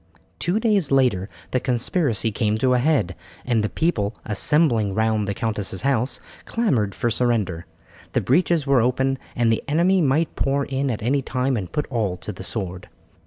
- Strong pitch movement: No, average, 4.7 semitones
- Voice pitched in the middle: No, low, 125 Hz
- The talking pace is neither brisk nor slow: Yes, average, 175 wpm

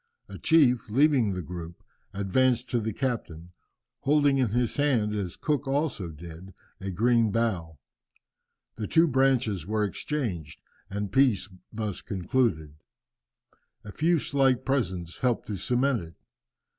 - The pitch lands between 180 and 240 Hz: No, low, 115 Hz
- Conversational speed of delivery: No, slow, 130 wpm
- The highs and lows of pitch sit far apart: Yes, wide, 5.9 semitones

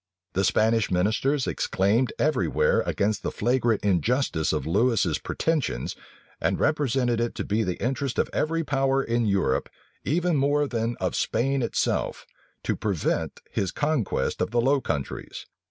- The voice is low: Yes, low, 120 Hz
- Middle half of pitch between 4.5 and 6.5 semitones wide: Yes, average, 5.0 semitones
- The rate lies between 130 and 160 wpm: Yes, average, 150 wpm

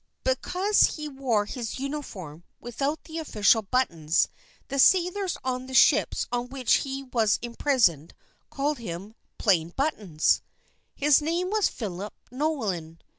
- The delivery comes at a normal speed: No, slow, 125 wpm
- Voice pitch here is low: No, very high, 255 Hz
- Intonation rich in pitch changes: Yes, wide, 6.5 semitones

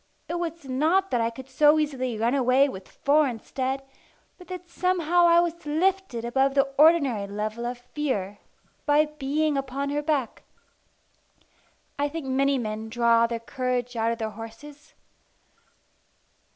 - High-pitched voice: Yes, very high, 270 Hz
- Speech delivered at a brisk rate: No, average, 150 wpm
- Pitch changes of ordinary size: Yes, average, 4.4 semitones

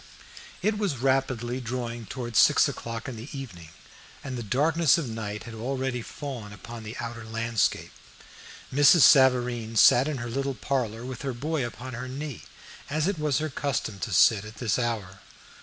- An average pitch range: Yes, average, 3.2 semitones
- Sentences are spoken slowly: No, average, 175 wpm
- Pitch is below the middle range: Yes, low, 125 Hz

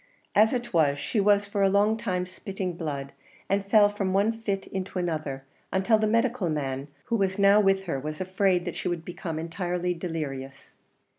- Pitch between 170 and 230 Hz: Yes, medium, 185 Hz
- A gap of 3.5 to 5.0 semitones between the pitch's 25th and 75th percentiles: Yes, average, 3.8 semitones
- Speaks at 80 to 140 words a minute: No, average, 190 wpm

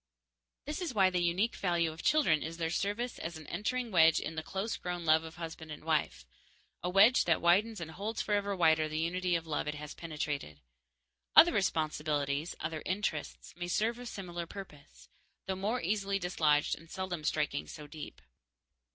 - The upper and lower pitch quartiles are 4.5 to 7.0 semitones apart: No, average, 3.9 semitones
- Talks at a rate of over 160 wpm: Yes, average, 185 wpm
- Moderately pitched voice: Yes, medium, 170 Hz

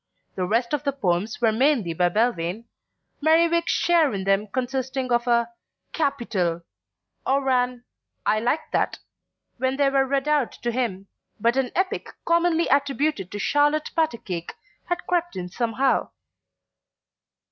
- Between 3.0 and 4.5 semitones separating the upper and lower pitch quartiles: No, average, 5.2 semitones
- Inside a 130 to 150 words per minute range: Yes, average, 140 wpm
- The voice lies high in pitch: Yes, very high, 255 Hz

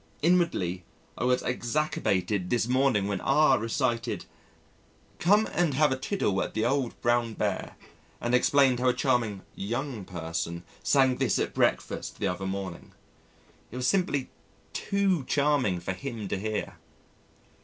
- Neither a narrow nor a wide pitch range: No, wide, 5.8 semitones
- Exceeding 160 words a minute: No, average, 145 wpm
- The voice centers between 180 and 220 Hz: No, low, 120 Hz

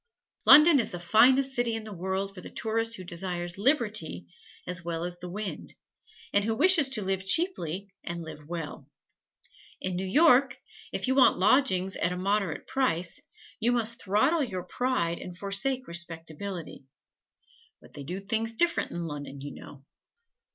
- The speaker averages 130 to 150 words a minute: No, average, 165 wpm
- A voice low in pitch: No, high, 195 Hz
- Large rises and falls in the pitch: Yes, wide, 5.7 semitones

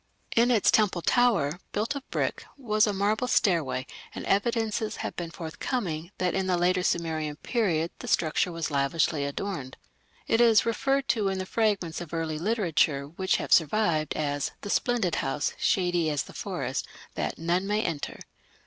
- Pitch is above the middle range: No, medium, 180 Hz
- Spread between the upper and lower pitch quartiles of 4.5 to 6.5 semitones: Yes, average, 5.3 semitones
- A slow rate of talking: No, average, 165 wpm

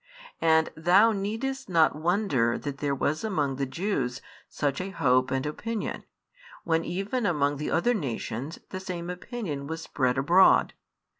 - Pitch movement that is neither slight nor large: No, wide, 5.7 semitones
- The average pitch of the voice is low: No, medium, 160 Hz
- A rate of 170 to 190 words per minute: No, average, 150 wpm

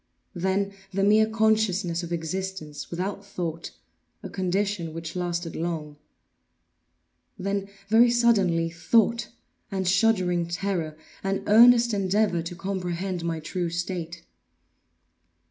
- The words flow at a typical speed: No, slow, 105 wpm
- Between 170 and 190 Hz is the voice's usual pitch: Yes, medium, 185 Hz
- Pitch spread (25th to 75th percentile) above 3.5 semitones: No, average, 2.9 semitones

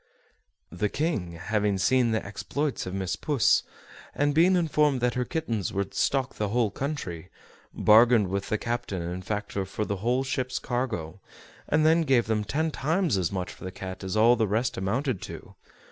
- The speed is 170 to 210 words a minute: Yes, average, 180 wpm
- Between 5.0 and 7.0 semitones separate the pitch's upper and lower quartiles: Yes, wide, 5.6 semitones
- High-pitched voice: No, low, 110 Hz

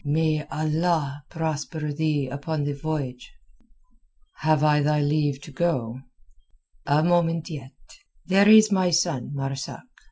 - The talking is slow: Yes, slow, 125 wpm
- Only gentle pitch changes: Yes, narrow, 2.3 semitones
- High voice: No, medium, 150 Hz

